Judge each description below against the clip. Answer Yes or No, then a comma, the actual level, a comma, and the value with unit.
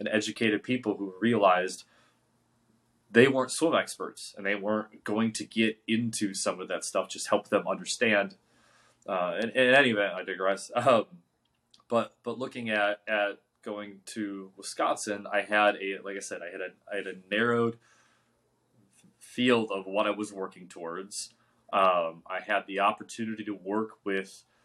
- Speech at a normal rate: Yes, average, 160 wpm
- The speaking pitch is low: Yes, low, 105 Hz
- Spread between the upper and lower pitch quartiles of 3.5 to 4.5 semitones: No, narrow, 2.6 semitones